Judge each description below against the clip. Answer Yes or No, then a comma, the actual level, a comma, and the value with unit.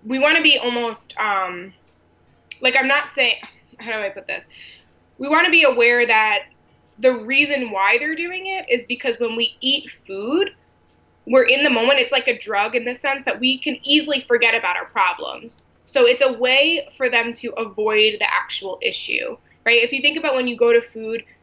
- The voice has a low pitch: No, very high, 255 Hz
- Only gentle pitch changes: No, average, 3.7 semitones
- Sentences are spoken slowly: No, fast, 205 wpm